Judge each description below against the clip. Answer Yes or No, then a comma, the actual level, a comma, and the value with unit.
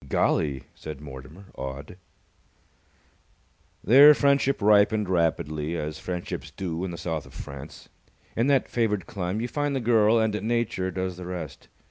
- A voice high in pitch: No, very low, 90 Hz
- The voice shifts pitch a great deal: Yes, wide, 6.3 semitones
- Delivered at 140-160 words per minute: Yes, average, 145 wpm